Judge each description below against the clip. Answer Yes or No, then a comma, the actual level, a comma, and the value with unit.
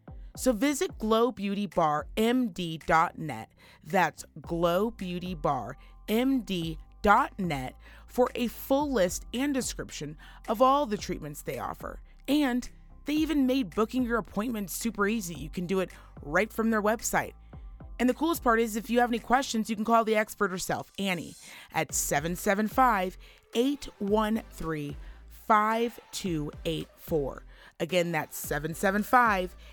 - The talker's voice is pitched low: No, high, 210 Hz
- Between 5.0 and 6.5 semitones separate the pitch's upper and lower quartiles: Yes, wide, 5.5 semitones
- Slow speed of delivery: Yes, slow, 120 wpm